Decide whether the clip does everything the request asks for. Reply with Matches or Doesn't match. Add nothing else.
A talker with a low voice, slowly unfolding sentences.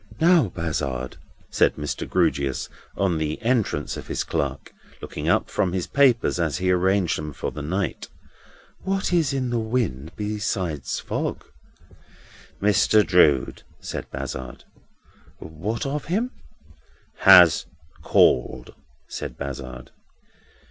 Matches